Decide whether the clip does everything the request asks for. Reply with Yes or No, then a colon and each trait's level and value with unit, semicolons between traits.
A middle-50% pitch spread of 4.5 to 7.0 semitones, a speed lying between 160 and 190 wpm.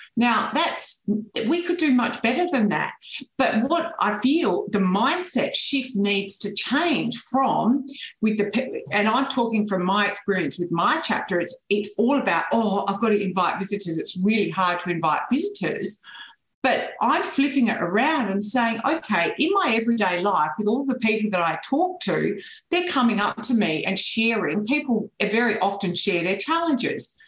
Yes: average, 5.1 semitones; average, 175 wpm